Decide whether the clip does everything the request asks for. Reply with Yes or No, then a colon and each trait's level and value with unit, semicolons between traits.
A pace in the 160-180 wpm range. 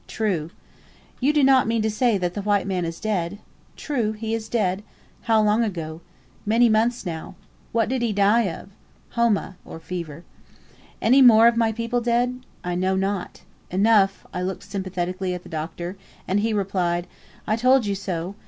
Yes: average, 170 wpm